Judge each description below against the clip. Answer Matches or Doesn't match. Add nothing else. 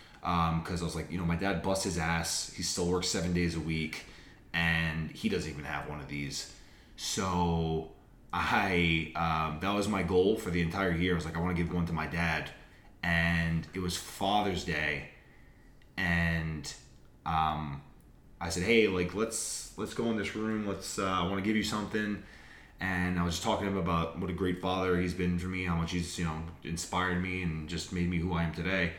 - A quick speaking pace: Matches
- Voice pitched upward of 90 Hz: Doesn't match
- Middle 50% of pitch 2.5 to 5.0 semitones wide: Doesn't match